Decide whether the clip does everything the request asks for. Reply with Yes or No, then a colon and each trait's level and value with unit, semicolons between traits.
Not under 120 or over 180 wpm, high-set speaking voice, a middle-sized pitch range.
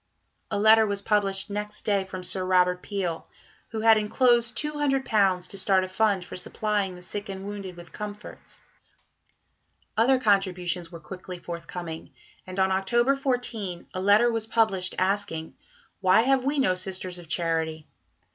Yes: average, 155 wpm; high, 195 Hz; average, 3.2 semitones